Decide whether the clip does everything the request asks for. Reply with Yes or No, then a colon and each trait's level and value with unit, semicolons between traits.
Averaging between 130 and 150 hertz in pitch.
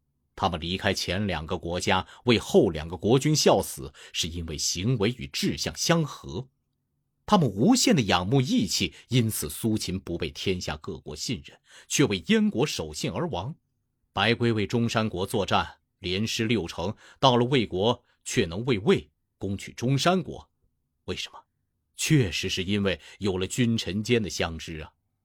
No: low, 105 Hz